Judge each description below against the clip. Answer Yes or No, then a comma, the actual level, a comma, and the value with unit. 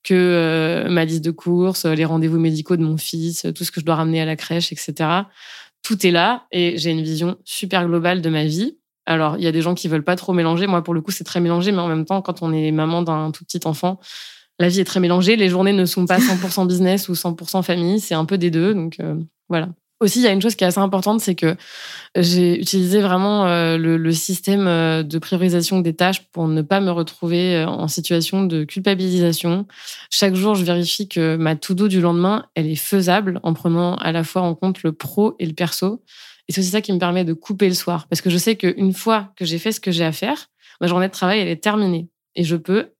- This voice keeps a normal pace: No, fast, 250 wpm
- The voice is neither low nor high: Yes, medium, 175 Hz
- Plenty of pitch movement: No, narrow, 2.4 semitones